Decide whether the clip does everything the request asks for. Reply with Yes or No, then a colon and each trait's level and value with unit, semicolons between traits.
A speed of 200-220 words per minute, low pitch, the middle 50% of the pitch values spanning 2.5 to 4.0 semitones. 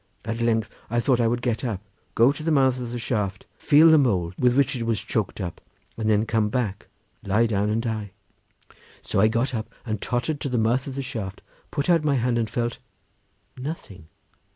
Yes: fast, 205 wpm; low, 115 Hz; average, 3.1 semitones